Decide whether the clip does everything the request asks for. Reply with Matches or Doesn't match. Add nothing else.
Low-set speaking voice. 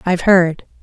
Doesn't match